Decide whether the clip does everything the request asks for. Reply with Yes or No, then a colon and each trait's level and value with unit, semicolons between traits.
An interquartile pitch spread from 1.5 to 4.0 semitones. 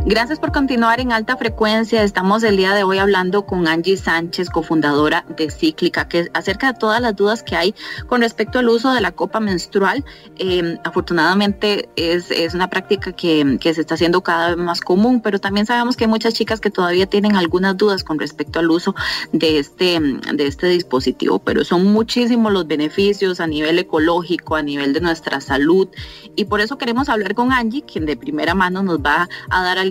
No: average, 4.8 semitones